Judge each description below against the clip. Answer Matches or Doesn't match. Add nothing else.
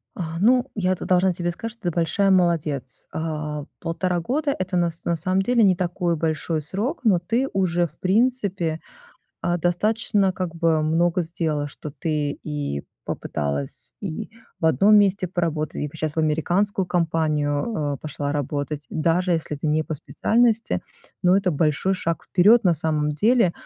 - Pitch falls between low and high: Matches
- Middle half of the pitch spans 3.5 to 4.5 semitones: Matches